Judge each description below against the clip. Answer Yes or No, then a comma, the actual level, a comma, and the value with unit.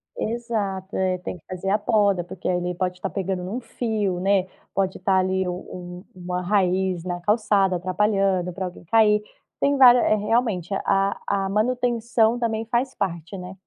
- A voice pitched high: Yes, high, 195 Hz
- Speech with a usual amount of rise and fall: Yes, average, 3.1 semitones